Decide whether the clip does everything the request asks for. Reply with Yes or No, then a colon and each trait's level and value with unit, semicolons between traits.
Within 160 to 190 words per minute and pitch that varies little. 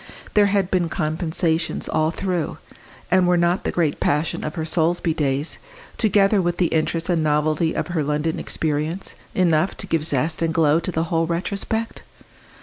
Yes: average, 170 wpm; narrow, 2.3 semitones